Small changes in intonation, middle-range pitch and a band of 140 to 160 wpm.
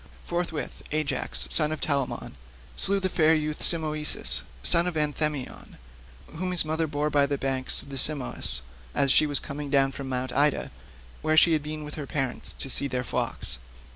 No: narrow, 2.3 semitones; medium, 150 Hz; average, 180 wpm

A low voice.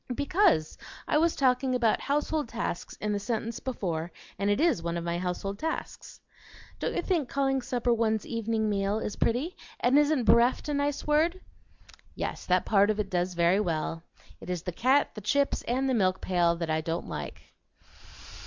No: high, 225 Hz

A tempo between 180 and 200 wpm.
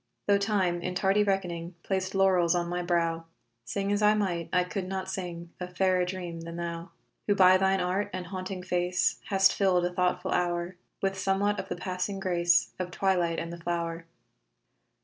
Yes: average, 185 wpm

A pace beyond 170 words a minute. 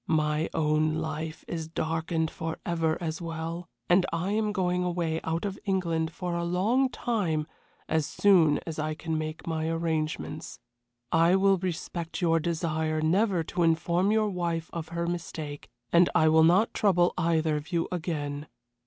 No: average, 160 wpm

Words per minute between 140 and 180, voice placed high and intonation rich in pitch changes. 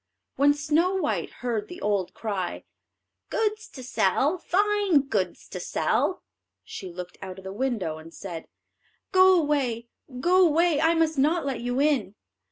Yes: average, 155 wpm; very high, 275 Hz; wide, 8.8 semitones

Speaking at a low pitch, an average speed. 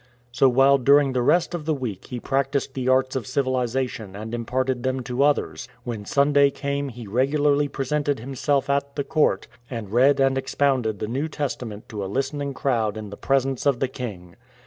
Yes: low, 130 Hz; average, 190 wpm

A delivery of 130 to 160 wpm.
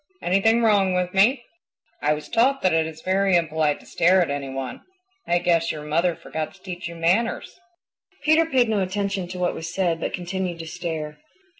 No: average, 195 wpm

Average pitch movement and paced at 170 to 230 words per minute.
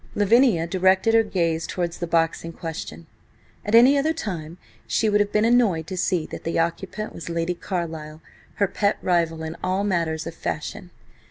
Yes: average, 3.9 semitones; average, 180 wpm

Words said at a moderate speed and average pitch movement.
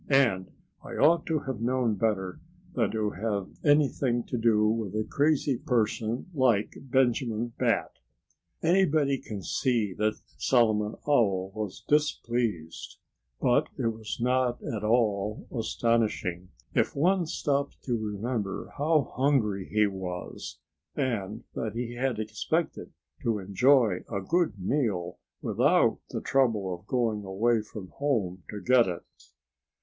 No: slow, 130 wpm; average, 4.2 semitones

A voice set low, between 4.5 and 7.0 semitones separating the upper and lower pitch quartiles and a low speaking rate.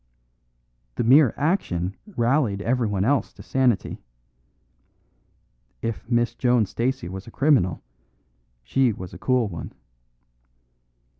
Yes: low, 120 Hz; average, 4.8 semitones; slow, 105 wpm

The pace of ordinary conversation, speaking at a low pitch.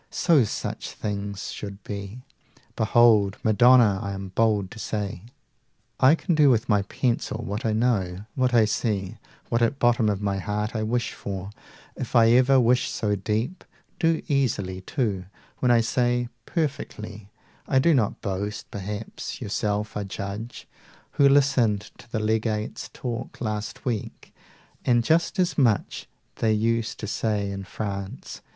Yes: average, 155 wpm; low, 110 Hz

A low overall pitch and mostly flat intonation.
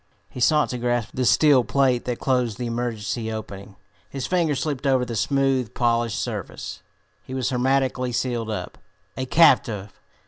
Yes: low, 125 Hz; narrow, 2.3 semitones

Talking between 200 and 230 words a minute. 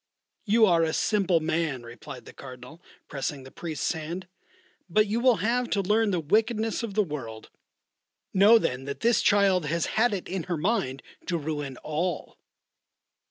No: average, 165 wpm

